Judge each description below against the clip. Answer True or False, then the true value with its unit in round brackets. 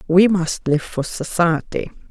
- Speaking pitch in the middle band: True (170 Hz)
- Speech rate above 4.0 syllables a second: False (3.9 syllables/s)